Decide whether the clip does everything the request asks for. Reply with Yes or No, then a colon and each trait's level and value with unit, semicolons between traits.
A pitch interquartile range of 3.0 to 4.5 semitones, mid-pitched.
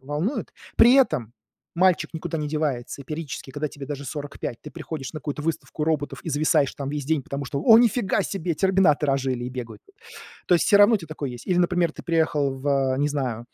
Yes: average, 3.5 semitones; medium, 150 Hz